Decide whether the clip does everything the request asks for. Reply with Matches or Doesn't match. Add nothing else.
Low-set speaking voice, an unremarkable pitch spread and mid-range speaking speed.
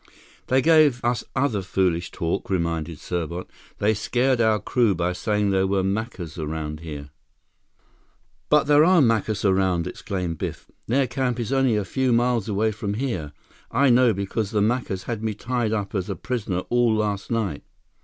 Matches